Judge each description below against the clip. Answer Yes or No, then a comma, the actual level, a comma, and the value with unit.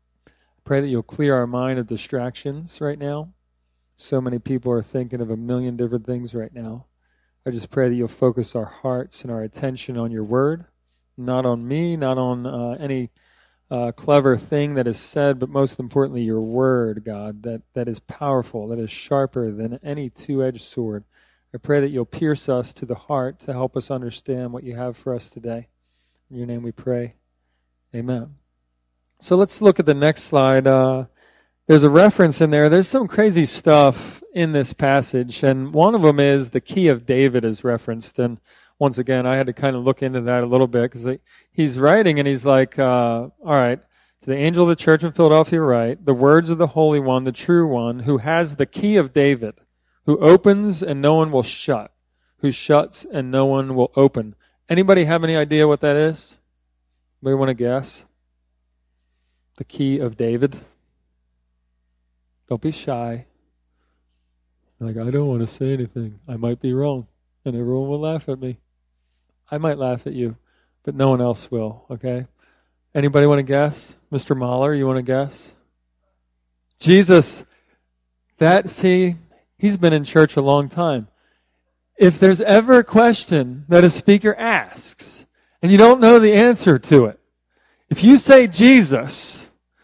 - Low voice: Yes, low, 130 Hz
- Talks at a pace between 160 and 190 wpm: Yes, average, 180 wpm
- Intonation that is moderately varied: Yes, average, 4.2 semitones